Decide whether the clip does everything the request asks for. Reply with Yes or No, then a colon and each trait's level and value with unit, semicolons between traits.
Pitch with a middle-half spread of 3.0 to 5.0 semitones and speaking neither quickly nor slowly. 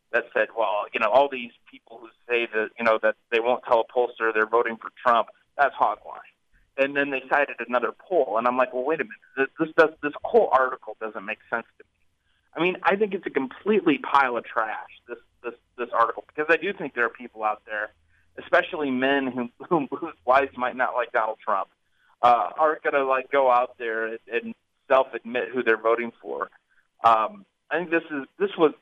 No: average, 3.6 semitones; fast, 215 wpm